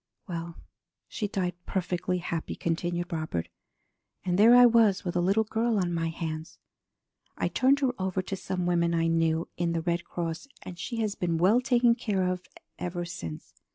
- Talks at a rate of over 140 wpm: Yes, average, 180 wpm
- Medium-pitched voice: Yes, medium, 180 Hz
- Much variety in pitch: No, average, 3.4 semitones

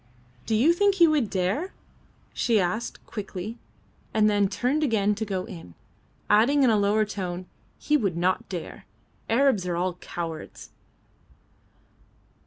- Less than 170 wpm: Yes, average, 140 wpm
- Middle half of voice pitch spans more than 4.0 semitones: Yes, average, 5.0 semitones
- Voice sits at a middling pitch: No, high, 210 Hz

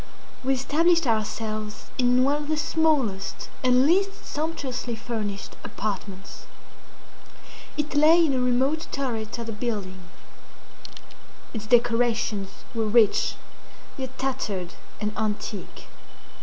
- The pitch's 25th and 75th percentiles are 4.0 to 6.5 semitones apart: Yes, average, 4.7 semitones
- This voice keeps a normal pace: No, slow, 110 wpm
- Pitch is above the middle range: Yes, high, 245 Hz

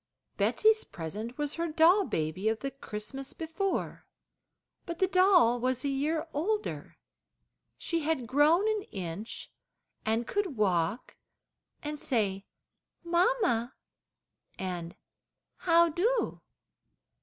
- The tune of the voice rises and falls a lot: Yes, wide, 7.7 semitones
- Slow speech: Yes, slow, 110 wpm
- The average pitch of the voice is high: Yes, very high, 290 Hz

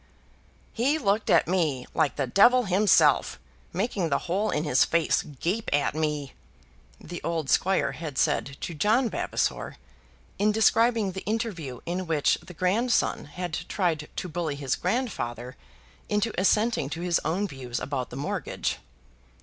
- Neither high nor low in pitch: Yes, medium, 175 Hz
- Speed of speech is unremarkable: Yes, average, 150 wpm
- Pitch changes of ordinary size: No, wide, 5.9 semitones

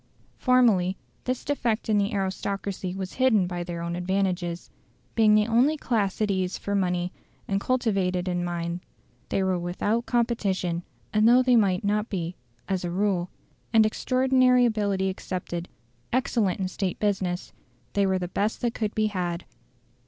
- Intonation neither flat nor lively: Yes, average, 3.6 semitones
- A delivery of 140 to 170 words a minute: Yes, average, 160 wpm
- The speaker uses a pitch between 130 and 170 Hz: No, high, 195 Hz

